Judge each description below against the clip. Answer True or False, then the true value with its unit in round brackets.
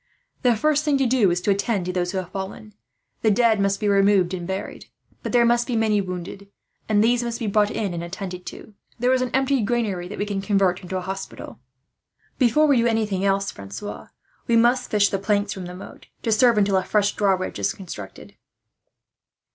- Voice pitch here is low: False (205 Hz)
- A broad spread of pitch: False (3.6 semitones)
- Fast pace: True (210 wpm)